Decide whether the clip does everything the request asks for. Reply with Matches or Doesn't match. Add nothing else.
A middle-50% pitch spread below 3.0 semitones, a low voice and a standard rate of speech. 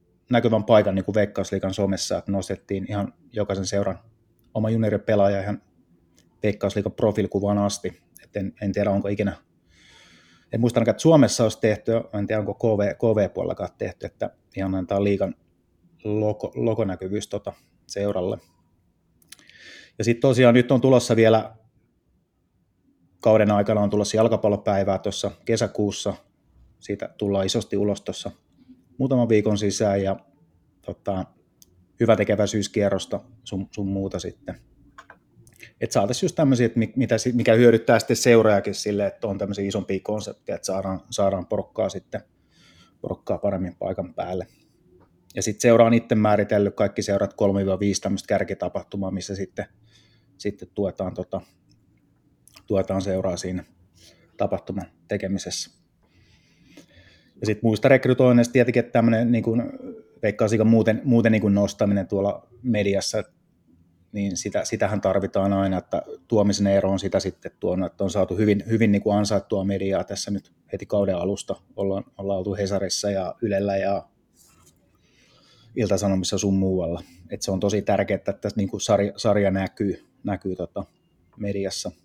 Matches